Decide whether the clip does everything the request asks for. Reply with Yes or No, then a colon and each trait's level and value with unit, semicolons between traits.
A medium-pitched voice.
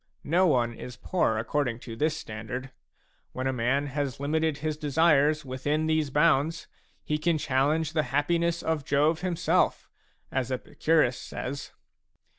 Yes: medium, 145 Hz